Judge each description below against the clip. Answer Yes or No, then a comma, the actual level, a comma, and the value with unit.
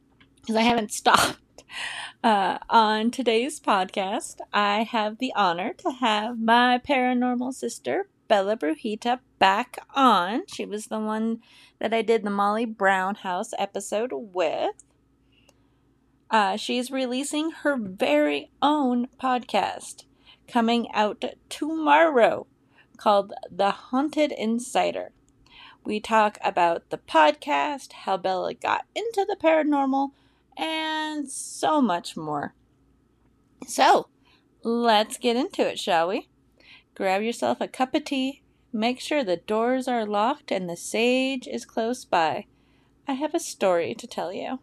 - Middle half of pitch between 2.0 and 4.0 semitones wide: No, average, 5.0 semitones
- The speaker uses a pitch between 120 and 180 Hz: No, high, 235 Hz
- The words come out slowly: Yes, slow, 125 wpm